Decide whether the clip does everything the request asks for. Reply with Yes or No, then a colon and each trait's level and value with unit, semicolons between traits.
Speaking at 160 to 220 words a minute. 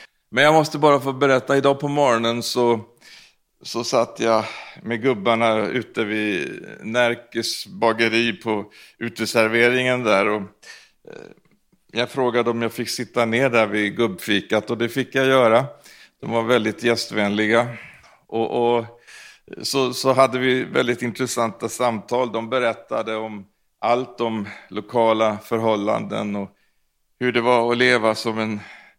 No: average, 135 wpm